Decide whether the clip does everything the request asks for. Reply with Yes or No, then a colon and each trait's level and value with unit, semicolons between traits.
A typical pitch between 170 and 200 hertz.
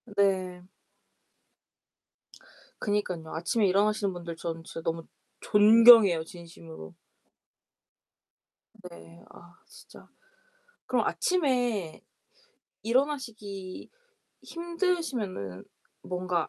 Yes: high, 190 Hz